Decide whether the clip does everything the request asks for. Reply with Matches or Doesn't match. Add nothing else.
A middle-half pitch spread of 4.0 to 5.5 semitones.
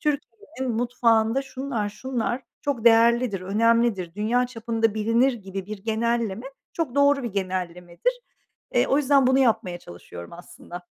Matches